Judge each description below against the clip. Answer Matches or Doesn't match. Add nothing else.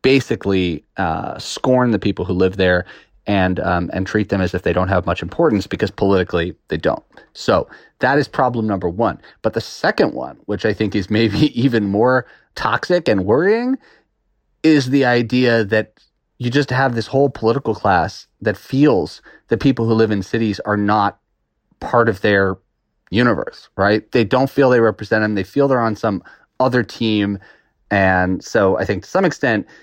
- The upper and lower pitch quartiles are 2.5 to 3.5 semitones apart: Doesn't match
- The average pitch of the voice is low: Matches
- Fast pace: Doesn't match